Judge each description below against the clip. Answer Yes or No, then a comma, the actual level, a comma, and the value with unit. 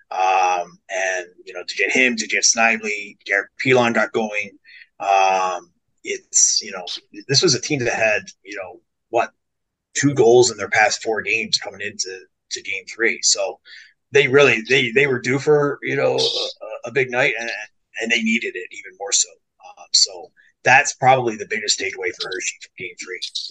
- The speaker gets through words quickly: No, average, 185 wpm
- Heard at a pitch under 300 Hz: No, very high, 370 Hz